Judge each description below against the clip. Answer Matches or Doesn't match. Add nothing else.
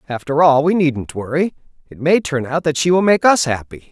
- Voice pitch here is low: Doesn't match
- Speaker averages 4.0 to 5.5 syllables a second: Matches